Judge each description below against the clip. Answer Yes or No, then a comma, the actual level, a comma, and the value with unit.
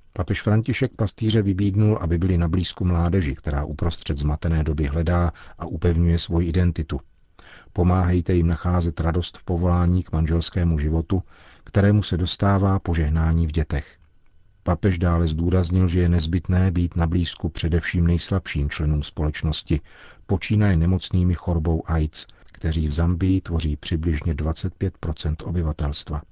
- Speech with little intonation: Yes, narrow, 2.2 semitones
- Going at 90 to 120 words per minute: No, average, 130 wpm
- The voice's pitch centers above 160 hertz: No, very low, 85 Hz